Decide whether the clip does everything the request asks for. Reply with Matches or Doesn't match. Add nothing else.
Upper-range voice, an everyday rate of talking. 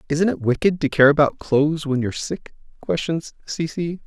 Doesn't match